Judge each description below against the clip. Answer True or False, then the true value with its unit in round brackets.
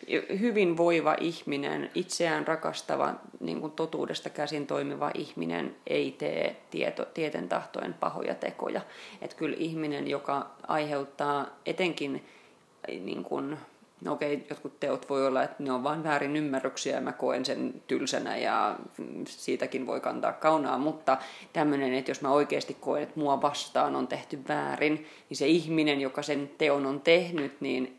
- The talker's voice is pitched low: False (145 Hz)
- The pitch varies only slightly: True (2.0 semitones)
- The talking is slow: False (150 wpm)